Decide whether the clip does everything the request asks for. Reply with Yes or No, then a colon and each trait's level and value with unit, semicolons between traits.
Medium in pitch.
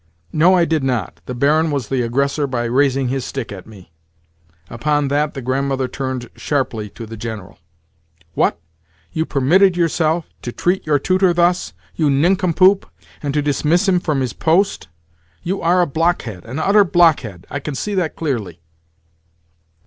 Yes: medium, 145 Hz